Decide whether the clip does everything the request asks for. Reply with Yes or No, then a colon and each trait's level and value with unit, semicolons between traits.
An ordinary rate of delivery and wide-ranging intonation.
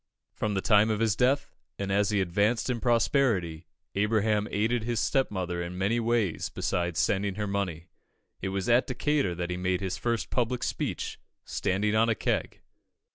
No: average, 175 wpm; average, 3.6 semitones